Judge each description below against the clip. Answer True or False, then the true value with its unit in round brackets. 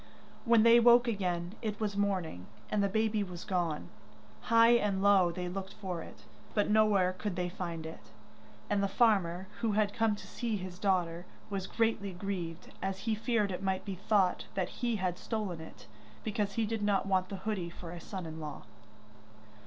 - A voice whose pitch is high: True (195 Hz)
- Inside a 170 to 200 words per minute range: True (190 wpm)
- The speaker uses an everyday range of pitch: True (3.0 semitones)